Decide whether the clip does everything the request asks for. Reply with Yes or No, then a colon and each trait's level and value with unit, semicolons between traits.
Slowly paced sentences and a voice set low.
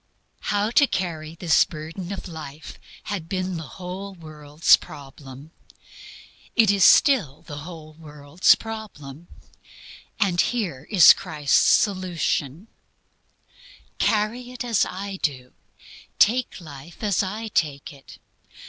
No: slow, 115 wpm; medium, 170 Hz